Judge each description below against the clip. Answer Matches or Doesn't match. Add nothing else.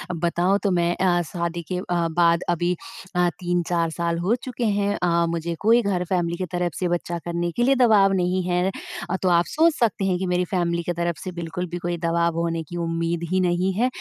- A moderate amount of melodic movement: Doesn't match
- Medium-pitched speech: Matches